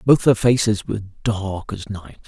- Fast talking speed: No, average, 185 wpm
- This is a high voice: No, low, 105 Hz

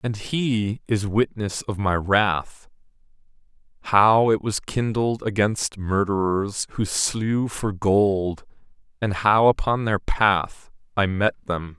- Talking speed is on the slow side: Yes, slow, 125 wpm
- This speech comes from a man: Yes, male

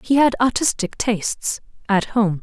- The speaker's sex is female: Yes, female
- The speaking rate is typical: No, slow, 125 wpm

